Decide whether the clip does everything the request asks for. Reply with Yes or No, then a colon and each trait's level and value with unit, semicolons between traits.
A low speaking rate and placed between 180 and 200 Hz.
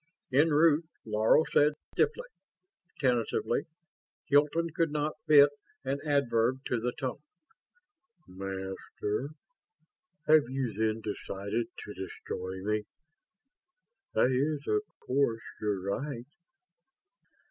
No: slow, 100 wpm; low, 130 Hz